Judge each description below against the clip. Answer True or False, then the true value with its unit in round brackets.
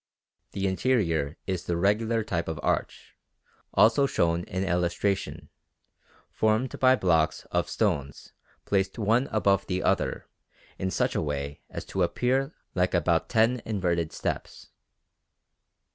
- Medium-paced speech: False (130 wpm)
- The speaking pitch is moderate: False (95 Hz)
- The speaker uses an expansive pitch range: False (4.7 semitones)